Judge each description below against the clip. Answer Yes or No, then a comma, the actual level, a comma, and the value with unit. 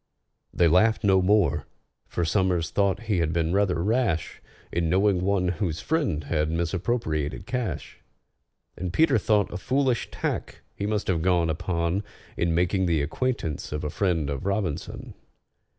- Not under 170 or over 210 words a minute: No, average, 150 wpm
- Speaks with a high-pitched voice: No, very low, 90 Hz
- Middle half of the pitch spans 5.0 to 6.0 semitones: No, average, 3.8 semitones